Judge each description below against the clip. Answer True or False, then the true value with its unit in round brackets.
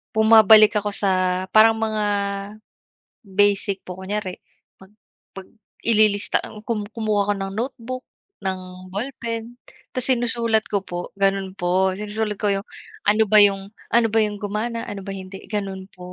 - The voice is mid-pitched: False (205 Hz)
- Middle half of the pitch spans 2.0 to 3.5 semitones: True (2.4 semitones)